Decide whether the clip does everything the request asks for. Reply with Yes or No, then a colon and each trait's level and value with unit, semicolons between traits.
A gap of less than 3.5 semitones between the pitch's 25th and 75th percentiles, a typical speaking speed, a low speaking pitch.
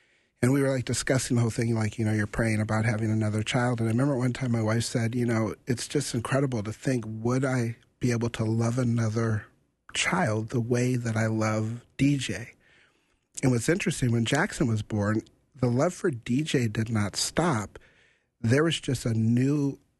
Yes: average, 2.8 semitones; average, 195 wpm; low, 120 Hz